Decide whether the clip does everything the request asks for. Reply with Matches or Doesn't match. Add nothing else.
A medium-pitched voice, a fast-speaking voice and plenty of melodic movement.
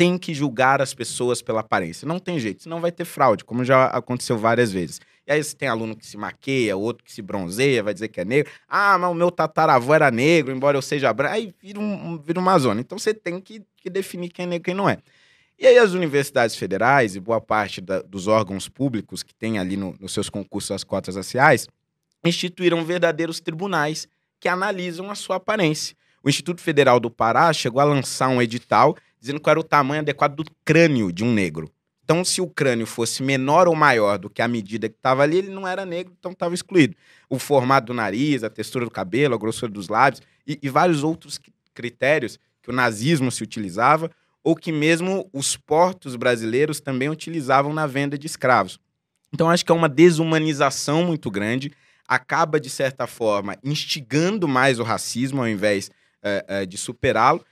Matches